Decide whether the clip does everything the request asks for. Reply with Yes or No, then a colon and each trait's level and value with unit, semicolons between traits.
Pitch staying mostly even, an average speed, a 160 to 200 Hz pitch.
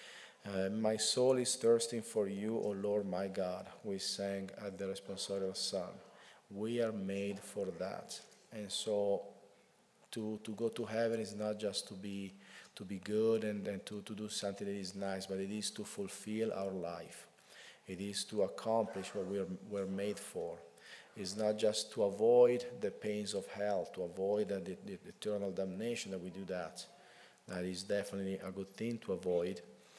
No: narrow, 1.9 semitones; average, 185 wpm; low, 100 Hz